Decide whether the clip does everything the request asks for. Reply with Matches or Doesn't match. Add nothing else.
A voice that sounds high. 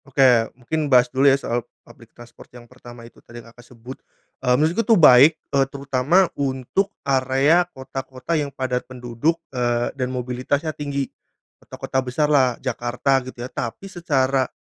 Doesn't match